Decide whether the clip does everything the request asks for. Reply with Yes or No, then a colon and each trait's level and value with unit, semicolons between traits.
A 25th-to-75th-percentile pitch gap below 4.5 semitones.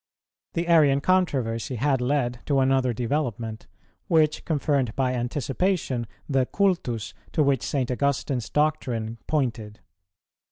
Yes: average, 3.7 semitones